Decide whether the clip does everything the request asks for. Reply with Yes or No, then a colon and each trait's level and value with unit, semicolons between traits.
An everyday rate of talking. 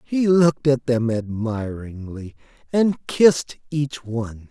No: slow, 120 wpm